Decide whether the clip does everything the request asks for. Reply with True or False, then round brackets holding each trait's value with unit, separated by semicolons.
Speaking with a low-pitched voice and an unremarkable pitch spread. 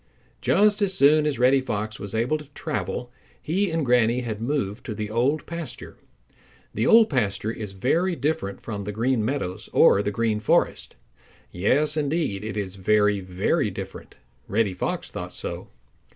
False (115 Hz; 6.2 semitones)